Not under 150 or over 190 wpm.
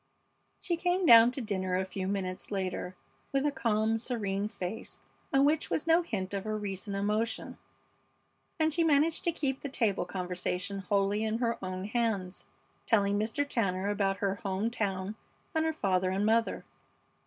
Yes: average, 165 wpm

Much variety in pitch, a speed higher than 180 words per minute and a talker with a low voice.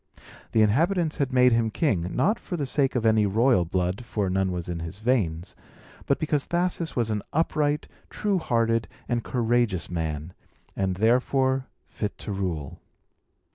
No: wide, 6.3 semitones; average, 160 wpm; low, 115 Hz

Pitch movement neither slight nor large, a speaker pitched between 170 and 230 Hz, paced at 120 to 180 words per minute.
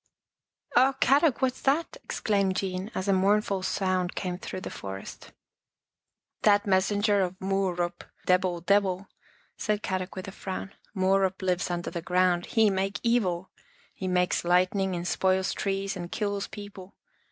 No: narrow, 1.9 semitones; high, 190 Hz; average, 165 wpm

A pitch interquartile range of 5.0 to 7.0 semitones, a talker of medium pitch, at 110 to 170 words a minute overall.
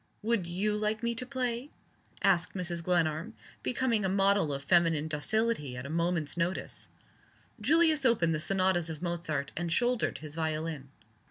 Yes: wide, 5.6 semitones; medium, 175 Hz; average, 155 wpm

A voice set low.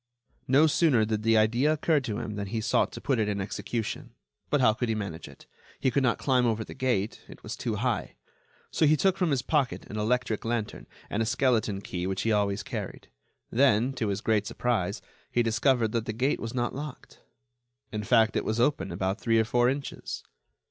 Yes: low, 115 Hz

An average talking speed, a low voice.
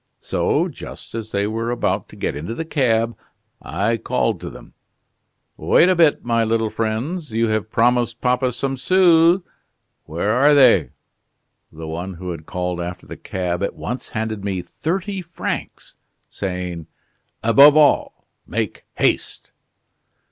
Yes: average, 145 wpm; low, 115 Hz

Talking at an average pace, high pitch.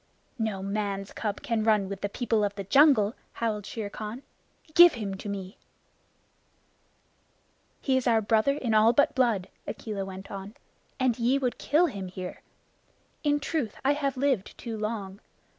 Yes: average, 160 wpm; high, 220 Hz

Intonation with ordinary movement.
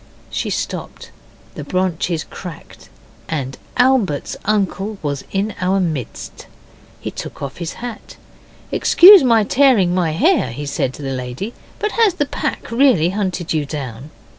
No: wide, 7.8 semitones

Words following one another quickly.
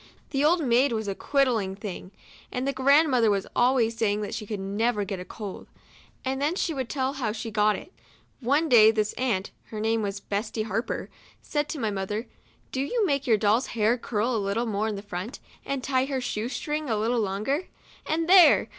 Yes: fast, 215 wpm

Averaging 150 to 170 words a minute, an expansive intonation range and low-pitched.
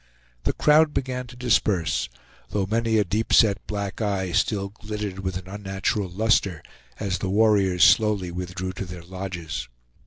No: average, 155 wpm; average, 2.7 semitones; low, 100 Hz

